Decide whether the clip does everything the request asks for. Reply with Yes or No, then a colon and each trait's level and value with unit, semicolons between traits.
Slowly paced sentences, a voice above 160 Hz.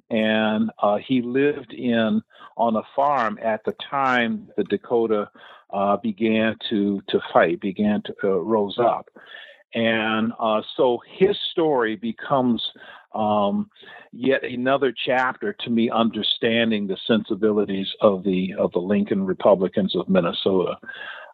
No: slow, 130 wpm; low, 110 Hz